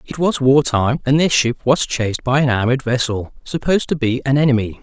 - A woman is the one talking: No, male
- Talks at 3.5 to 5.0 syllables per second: No, 5.5 syllables/s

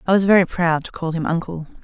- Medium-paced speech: No, fast, 260 wpm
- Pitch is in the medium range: Yes, medium, 170 Hz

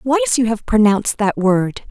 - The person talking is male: No, female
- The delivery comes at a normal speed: Yes, average, 190 wpm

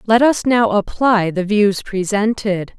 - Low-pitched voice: No, high, 210 Hz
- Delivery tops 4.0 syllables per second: No, 3.8 syllables/s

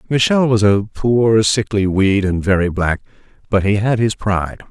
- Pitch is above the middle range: No, low, 105 Hz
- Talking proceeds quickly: No, average, 180 wpm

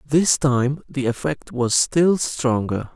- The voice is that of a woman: No, male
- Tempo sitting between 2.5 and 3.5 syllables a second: Yes, 3.2 syllables/s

